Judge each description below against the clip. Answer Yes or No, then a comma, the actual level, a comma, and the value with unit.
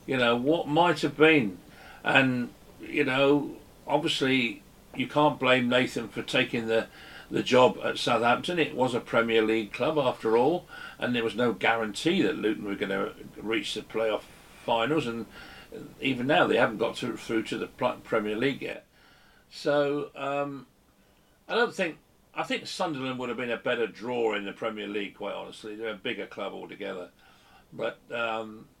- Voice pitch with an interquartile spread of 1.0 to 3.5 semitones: No, average, 4.5 semitones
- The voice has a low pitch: Yes, low, 125 Hz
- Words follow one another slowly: No, average, 175 wpm